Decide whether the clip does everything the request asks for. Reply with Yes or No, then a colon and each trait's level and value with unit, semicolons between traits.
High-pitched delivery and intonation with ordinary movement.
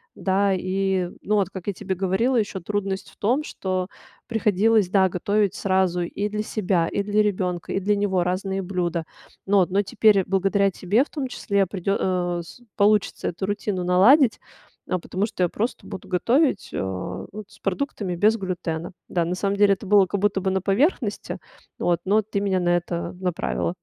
No: high, 195 Hz; narrow, 2.3 semitones